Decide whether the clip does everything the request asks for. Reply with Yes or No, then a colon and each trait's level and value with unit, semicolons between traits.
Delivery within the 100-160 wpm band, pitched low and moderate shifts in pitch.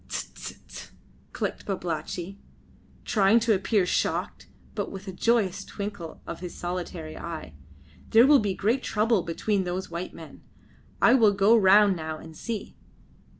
No: average, 150 wpm; high, 195 Hz; average, 3.5 semitones